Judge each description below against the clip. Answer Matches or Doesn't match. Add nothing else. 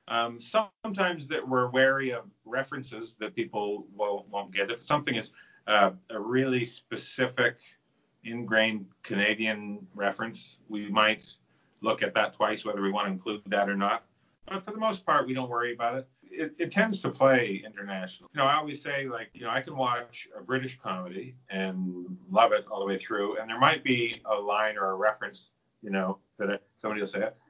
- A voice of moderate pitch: Doesn't match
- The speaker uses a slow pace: Doesn't match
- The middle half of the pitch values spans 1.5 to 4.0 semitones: Doesn't match